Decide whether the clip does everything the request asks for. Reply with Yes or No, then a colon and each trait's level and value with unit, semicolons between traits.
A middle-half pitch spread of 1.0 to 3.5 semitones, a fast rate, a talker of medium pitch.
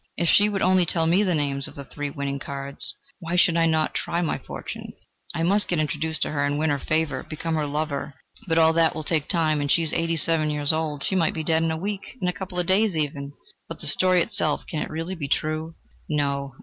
Yes: narrow, 2.5 semitones; fast, 250 wpm; medium, 160 Hz